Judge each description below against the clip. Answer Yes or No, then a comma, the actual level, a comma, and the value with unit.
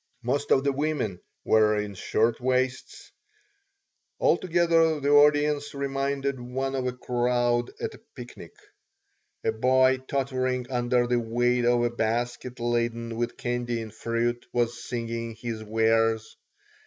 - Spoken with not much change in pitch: Yes, narrow, 2.3 semitones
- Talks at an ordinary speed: No, slow, 130 wpm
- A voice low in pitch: Yes, low, 120 Hz